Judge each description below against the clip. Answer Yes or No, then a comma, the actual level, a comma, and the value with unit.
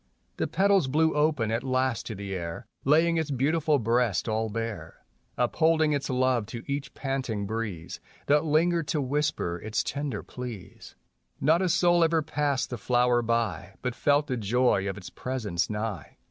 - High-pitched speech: No, low, 125 Hz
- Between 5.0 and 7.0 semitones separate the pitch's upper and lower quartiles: Yes, average, 5.3 semitones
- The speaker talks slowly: No, average, 165 wpm